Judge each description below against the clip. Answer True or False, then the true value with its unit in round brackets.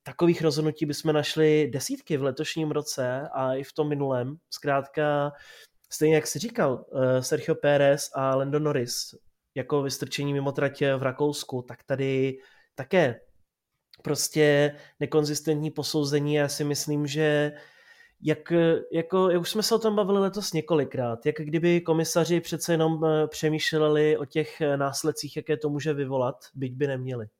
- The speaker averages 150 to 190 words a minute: False (140 wpm)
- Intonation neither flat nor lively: False (2.0 semitones)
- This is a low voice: False (150 Hz)